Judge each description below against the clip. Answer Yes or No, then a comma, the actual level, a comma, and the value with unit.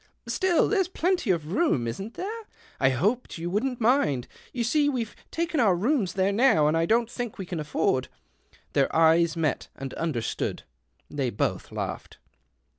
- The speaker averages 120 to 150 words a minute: No, average, 175 wpm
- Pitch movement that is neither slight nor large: No, wide, 9.0 semitones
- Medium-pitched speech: No, high, 195 Hz